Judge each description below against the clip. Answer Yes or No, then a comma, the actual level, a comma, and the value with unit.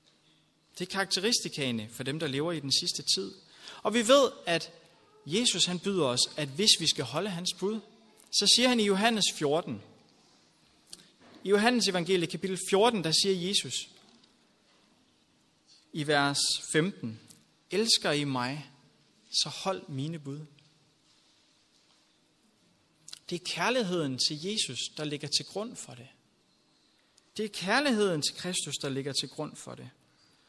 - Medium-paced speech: No, slow, 140 wpm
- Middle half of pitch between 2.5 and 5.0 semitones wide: No, wide, 5.5 semitones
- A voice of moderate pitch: Yes, medium, 165 Hz